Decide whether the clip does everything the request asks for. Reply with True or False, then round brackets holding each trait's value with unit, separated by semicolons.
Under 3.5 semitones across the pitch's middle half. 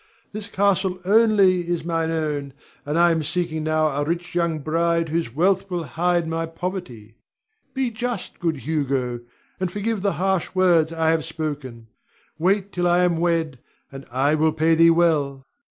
True (2.8 semitones)